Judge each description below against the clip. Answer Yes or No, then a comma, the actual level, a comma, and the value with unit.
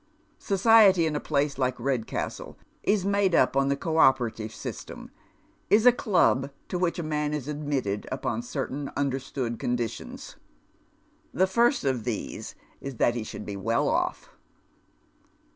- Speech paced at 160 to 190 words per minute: No, average, 150 wpm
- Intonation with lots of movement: Yes, wide, 6.1 semitones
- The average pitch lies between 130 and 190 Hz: Yes, medium, 140 Hz